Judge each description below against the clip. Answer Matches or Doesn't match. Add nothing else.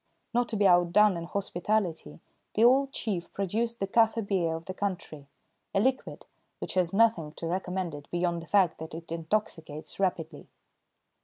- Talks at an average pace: Matches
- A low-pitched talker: Doesn't match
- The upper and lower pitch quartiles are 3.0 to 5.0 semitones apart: Matches